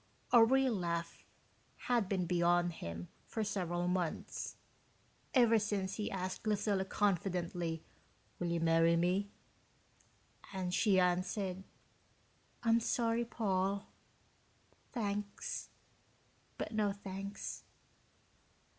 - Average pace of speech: No, slow, 95 wpm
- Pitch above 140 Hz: Yes, high, 190 Hz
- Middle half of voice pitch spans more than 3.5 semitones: No, average, 3.1 semitones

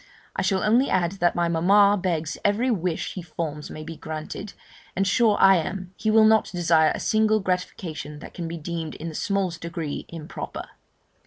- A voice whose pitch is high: No, medium, 175 Hz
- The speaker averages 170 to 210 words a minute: Yes, average, 185 wpm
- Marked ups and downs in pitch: No, average, 3.6 semitones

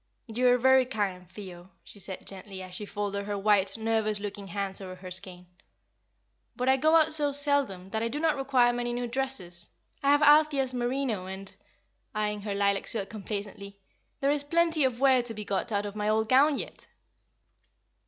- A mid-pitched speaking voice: No, high, 220 Hz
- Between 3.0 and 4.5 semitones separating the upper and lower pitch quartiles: No, average, 5.0 semitones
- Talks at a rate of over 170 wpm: Yes, average, 190 wpm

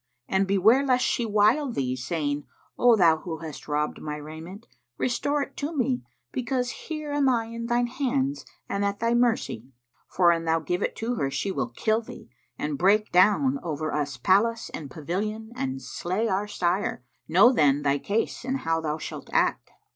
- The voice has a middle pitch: No, high, 200 Hz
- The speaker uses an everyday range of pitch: No, wide, 7.4 semitones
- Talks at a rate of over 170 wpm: Yes, average, 180 wpm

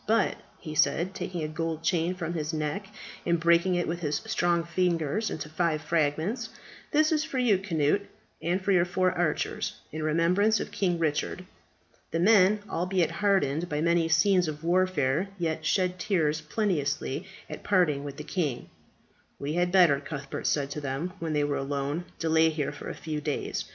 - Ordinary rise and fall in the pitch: Yes, average, 3.3 semitones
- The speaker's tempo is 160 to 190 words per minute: Yes, average, 175 wpm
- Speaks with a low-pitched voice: No, medium, 170 Hz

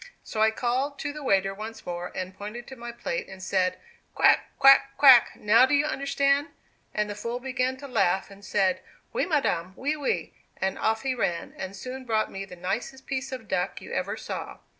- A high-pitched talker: Yes, high, 235 Hz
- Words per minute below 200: No, fast, 205 wpm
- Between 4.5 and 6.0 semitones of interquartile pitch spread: Yes, wide, 5.5 semitones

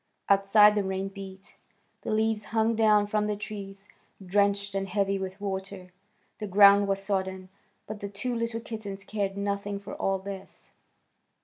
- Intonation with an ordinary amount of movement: No, narrow, 1.3 semitones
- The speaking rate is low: No, average, 155 wpm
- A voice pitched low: No, high, 200 Hz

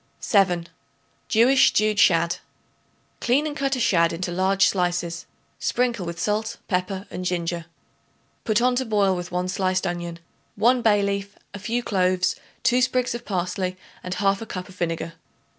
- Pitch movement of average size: Yes, average, 3.8 semitones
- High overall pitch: Yes, high, 195 Hz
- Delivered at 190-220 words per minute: No, average, 160 wpm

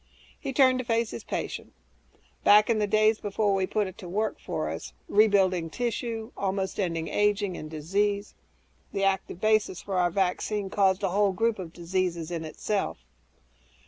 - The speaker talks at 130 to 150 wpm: No, average, 170 wpm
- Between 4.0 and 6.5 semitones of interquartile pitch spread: No, average, 2.7 semitones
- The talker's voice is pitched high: Yes, high, 200 Hz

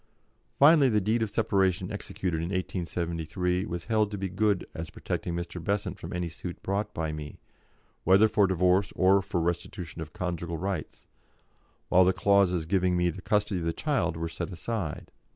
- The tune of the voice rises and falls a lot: No, average, 2.9 semitones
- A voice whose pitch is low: Yes, very low, 90 Hz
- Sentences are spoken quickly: No, average, 175 wpm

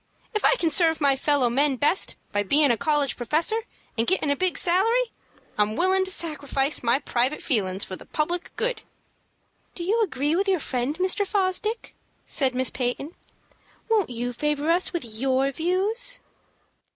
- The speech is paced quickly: No, average, 165 wpm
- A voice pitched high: Yes, very high, 300 Hz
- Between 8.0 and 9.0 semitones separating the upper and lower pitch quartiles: No, wide, 6.3 semitones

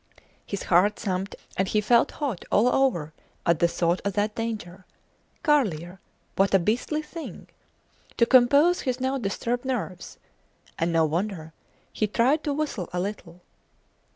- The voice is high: Yes, high, 210 Hz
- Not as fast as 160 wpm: Yes, average, 150 wpm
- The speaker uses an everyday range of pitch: No, wide, 6.1 semitones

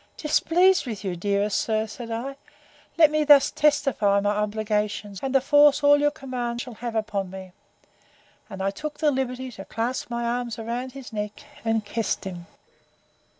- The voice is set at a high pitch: Yes, high, 235 Hz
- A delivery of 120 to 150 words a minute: No, average, 170 wpm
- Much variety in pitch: No, average, 4.7 semitones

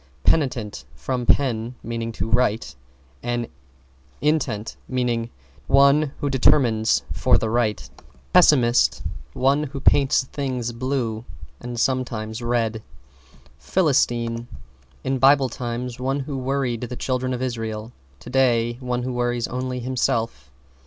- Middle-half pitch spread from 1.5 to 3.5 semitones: Yes, narrow, 2.4 semitones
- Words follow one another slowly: Yes, slow, 120 wpm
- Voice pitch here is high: No, low, 125 Hz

